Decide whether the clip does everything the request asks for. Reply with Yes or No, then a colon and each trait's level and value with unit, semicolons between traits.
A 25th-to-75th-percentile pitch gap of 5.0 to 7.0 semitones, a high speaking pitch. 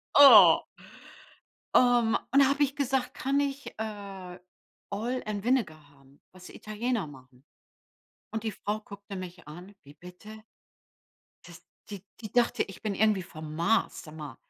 Yes: wide, 5.4 semitones; high, 205 Hz